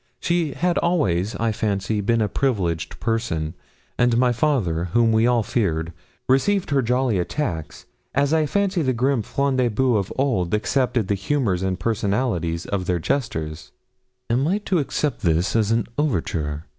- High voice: No, low, 115 Hz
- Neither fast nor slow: Yes, average, 165 wpm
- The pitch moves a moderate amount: No, wide, 6.6 semitones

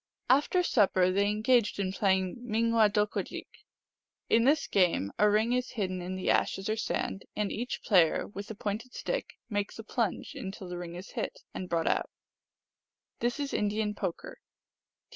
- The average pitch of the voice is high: Yes, high, 210 Hz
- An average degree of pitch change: Yes, average, 3.5 semitones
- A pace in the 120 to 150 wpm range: No, average, 165 wpm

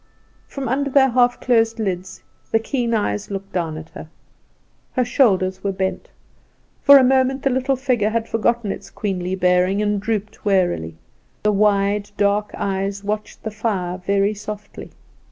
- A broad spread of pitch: No, average, 3.7 semitones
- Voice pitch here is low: No, high, 210 Hz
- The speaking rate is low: No, average, 155 wpm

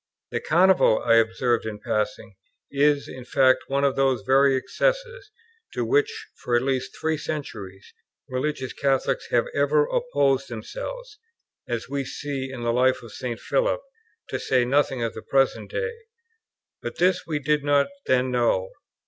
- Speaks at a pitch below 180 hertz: Yes, low, 135 Hz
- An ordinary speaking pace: Yes, average, 160 wpm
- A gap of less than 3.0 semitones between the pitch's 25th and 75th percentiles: No, average, 4.5 semitones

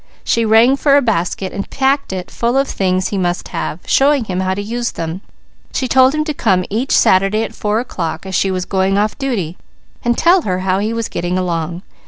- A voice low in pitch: No, high, 200 Hz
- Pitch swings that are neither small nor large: Yes, average, 4.8 semitones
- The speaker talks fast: Yes, fast, 220 wpm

